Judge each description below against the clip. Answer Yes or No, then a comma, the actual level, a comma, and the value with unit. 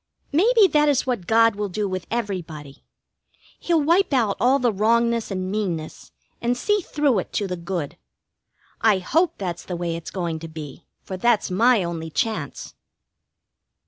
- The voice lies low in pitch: No, high, 205 Hz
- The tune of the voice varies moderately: No, wide, 6.0 semitones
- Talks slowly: No, average, 165 wpm